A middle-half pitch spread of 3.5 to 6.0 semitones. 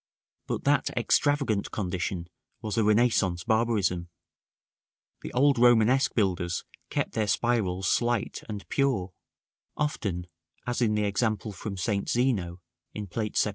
Yes: average, 4.2 semitones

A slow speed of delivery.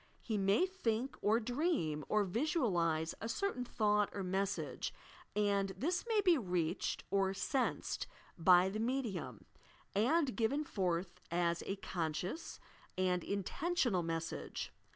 Yes: slow, 125 wpm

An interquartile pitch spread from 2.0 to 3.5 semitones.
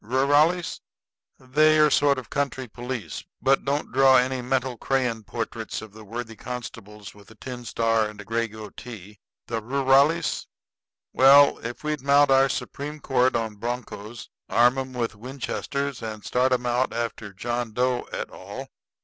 Yes: average, 3.0 semitones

